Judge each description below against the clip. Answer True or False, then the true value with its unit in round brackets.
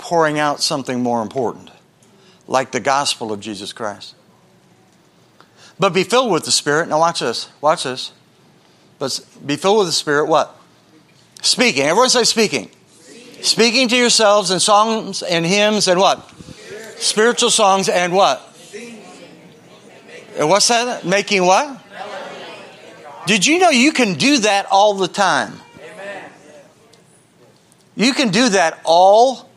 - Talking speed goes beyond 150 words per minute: False (135 wpm)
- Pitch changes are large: True (6.6 semitones)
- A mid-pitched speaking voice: False (195 Hz)